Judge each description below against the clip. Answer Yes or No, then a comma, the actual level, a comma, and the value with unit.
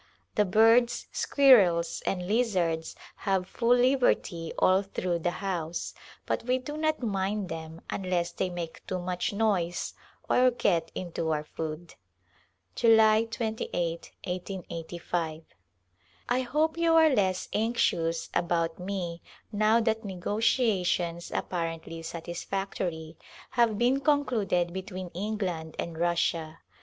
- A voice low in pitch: No, medium, 185 Hz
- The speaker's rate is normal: No, slow, 125 wpm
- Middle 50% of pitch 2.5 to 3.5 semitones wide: No, average, 4.8 semitones